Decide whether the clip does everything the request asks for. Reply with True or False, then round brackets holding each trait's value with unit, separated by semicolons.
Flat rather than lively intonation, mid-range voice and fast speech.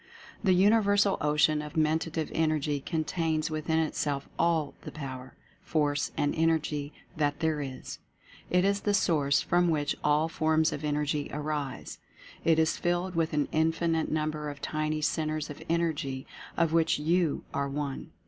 False (1.8 semitones; 155 Hz; 155 wpm)